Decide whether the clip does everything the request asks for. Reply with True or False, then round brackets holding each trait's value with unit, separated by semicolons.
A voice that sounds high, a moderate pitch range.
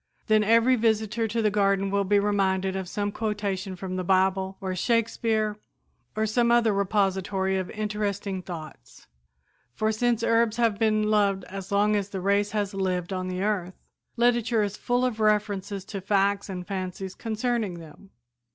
False (205 Hz; 2.3 semitones)